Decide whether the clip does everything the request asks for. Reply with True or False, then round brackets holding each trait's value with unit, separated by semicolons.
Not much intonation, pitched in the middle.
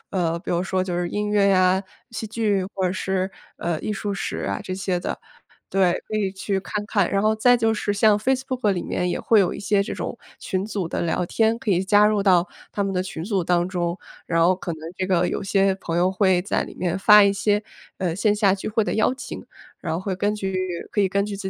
False (2.3 semitones; 195 Hz)